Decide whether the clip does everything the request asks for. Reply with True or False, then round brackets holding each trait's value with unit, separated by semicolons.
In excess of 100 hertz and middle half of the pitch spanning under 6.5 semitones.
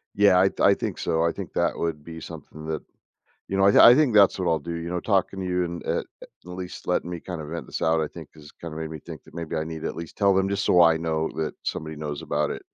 False (85 Hz; 2.8 semitones)